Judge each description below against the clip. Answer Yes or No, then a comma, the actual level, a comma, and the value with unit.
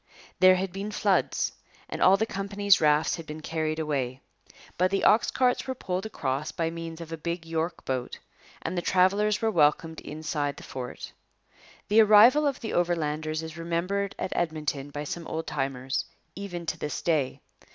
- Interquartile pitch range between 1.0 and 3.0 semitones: No, average, 4.2 semitones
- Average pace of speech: Yes, average, 175 wpm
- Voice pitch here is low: No, medium, 165 Hz